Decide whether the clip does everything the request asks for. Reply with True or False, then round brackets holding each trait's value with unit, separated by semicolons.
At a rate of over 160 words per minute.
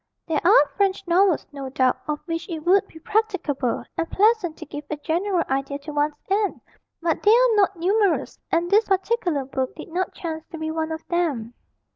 True (195 wpm)